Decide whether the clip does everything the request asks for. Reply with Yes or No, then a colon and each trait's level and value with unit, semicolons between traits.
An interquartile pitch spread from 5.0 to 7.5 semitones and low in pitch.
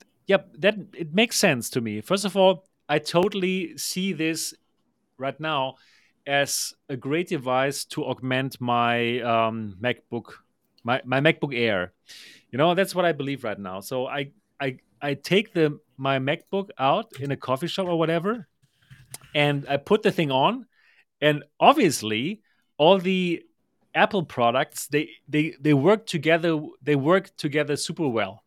No: wide, 5.4 semitones; medium, 150 Hz